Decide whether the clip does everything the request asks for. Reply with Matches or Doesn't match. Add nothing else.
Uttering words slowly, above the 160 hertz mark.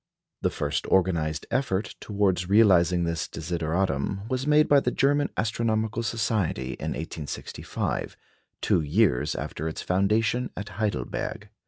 Doesn't match